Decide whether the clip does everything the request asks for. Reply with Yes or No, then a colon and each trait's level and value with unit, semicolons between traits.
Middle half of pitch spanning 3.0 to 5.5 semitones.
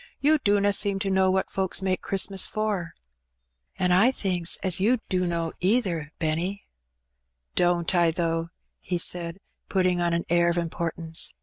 No: narrow, 2.4 semitones